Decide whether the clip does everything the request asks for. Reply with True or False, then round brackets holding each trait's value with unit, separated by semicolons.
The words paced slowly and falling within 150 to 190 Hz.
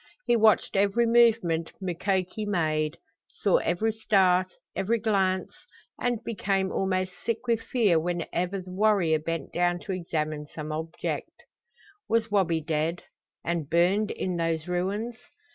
True (130 wpm; 185 Hz)